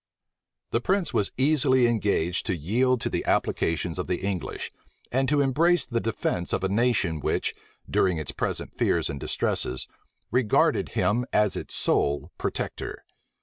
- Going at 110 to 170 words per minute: Yes, average, 150 wpm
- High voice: No, low, 110 Hz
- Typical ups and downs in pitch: No, wide, 6.4 semitones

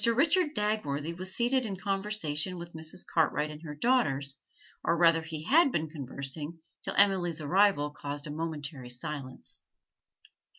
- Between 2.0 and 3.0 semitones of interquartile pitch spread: No, average, 5.1 semitones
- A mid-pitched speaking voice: Yes, medium, 165 Hz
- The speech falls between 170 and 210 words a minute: No, average, 140 wpm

